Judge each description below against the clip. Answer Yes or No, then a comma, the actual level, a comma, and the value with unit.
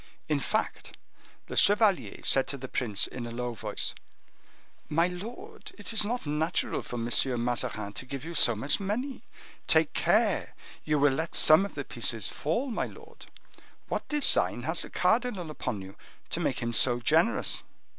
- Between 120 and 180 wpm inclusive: Yes, average, 170 wpm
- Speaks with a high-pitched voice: No, medium, 150 Hz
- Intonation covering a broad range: Yes, wide, 9.0 semitones